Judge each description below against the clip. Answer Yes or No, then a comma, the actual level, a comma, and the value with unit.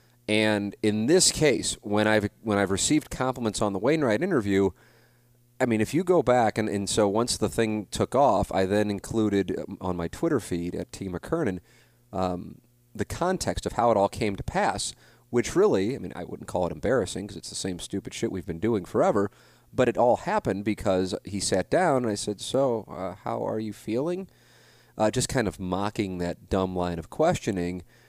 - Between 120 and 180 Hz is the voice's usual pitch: No, low, 105 Hz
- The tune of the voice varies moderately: Yes, average, 3.6 semitones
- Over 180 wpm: Yes, average, 200 wpm